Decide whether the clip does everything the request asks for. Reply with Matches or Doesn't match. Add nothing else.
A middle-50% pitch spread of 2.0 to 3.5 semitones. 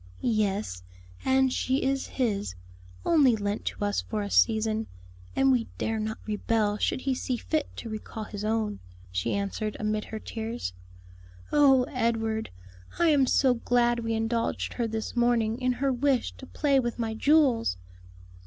Matches